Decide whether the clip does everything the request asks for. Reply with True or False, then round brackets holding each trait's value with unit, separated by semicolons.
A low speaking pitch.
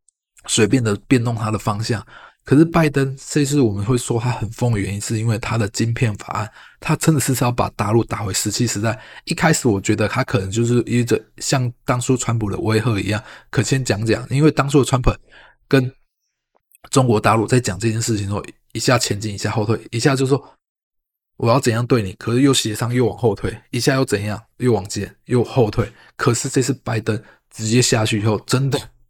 True (120 Hz)